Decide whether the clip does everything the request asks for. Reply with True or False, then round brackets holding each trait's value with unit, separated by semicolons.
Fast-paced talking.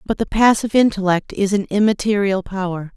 False (160 wpm)